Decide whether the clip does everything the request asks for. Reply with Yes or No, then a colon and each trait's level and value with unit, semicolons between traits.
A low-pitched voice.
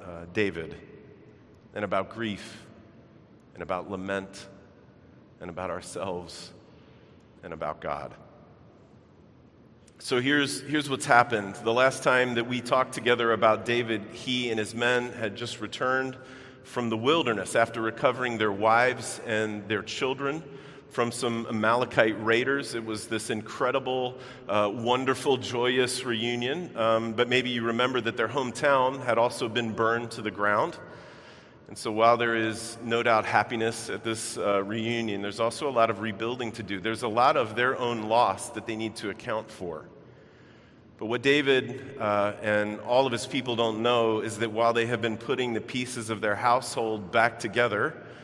Yes: low, 115 Hz